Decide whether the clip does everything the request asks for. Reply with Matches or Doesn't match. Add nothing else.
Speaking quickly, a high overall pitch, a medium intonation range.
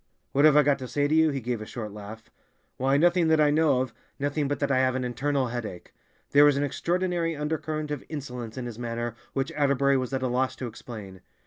Doesn't match